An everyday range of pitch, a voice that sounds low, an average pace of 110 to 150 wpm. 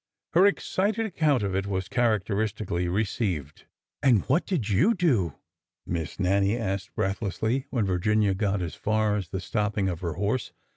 No: average, 4.1 semitones; low, 105 Hz; average, 165 wpm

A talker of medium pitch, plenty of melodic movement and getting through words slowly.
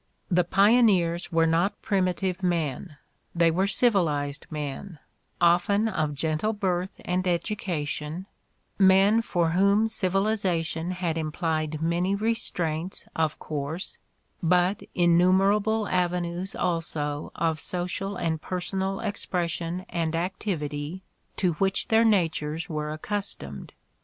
No: medium, 175 Hz; average, 3.2 semitones; slow, 105 wpm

